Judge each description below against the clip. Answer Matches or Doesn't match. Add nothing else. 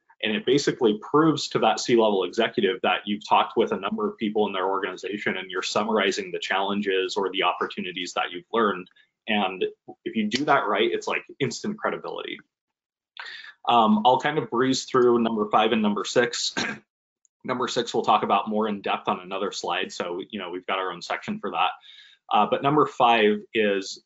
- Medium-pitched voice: Doesn't match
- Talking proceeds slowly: Doesn't match